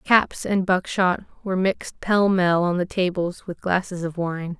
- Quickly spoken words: No, average, 185 wpm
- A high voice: No, medium, 180 Hz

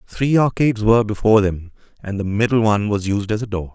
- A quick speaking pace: Yes, fast, 225 wpm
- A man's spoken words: Yes, male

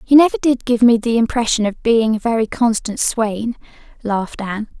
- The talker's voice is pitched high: Yes, high, 230 Hz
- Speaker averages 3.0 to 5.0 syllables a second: No, 5.4 syllables/s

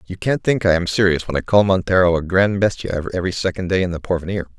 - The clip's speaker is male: Yes, male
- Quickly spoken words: Yes, fast, 250 wpm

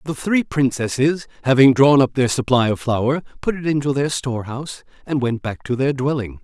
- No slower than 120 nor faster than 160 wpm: No, average, 195 wpm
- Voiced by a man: Yes, male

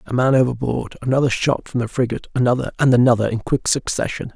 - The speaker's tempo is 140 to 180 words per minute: Yes, average, 165 wpm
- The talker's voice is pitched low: Yes, low, 125 Hz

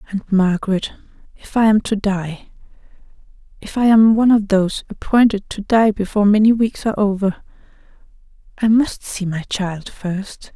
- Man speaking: No, female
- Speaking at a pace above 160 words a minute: No, average, 140 wpm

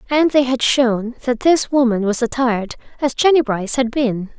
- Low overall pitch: No, very high, 250 Hz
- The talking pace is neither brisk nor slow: Yes, average, 190 wpm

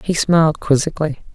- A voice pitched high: No, medium, 155 Hz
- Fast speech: No, slow, 135 wpm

